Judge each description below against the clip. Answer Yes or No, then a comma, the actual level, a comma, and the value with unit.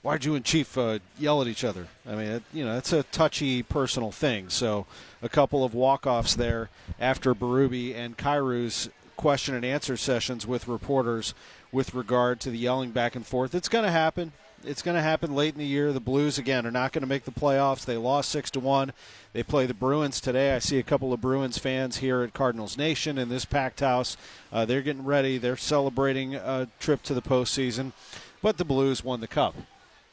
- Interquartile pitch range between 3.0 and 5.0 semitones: No, narrow, 2.4 semitones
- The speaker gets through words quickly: Yes, fast, 210 wpm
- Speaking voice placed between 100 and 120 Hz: No, low, 130 Hz